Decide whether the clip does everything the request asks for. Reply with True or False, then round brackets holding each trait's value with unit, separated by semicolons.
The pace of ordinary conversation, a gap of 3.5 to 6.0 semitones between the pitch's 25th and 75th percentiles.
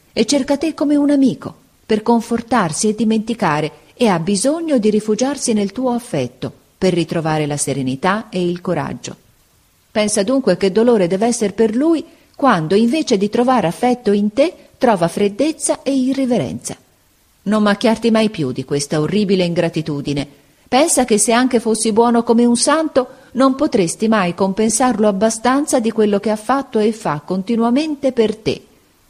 True (155 wpm; 5.5 semitones)